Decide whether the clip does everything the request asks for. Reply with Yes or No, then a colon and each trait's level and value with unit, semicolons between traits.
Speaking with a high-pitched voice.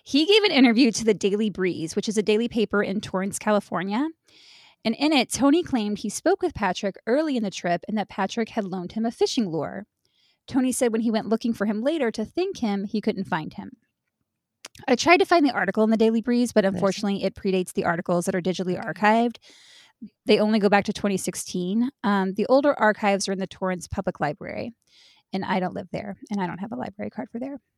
Yes: high, 215 Hz